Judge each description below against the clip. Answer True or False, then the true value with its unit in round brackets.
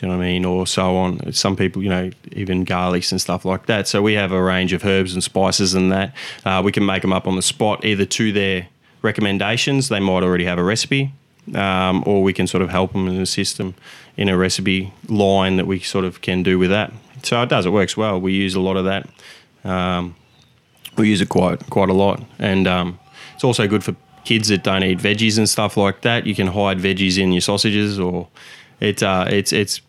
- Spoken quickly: True (240 wpm)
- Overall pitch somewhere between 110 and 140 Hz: False (95 Hz)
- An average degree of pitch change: False (1.9 semitones)